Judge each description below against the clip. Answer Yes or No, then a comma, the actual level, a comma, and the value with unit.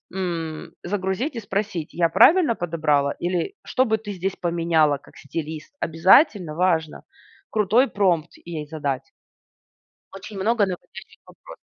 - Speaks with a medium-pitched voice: Yes, medium, 175 Hz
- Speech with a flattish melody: No, average, 4.1 semitones